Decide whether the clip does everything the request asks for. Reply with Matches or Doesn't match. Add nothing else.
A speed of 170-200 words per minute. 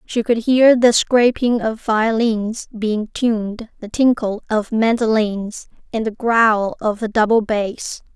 Doesn't match